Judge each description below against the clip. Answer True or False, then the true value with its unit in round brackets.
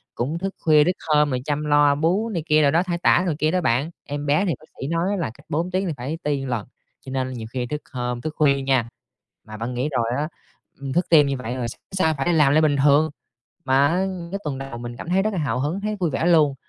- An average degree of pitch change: True (3.9 semitones)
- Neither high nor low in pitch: True (150 Hz)